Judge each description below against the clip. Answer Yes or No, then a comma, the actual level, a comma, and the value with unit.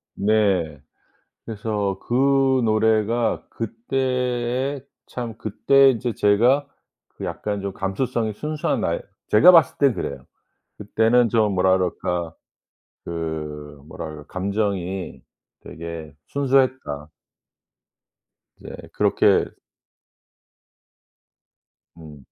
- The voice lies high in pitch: No, low, 110 Hz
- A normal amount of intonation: No, wide, 5.7 semitones